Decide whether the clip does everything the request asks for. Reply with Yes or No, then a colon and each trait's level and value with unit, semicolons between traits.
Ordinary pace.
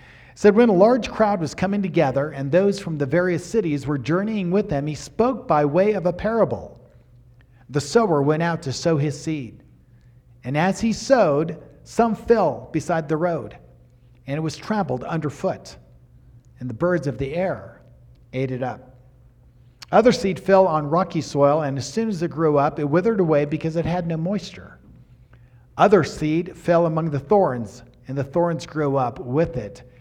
Yes: average, 180 wpm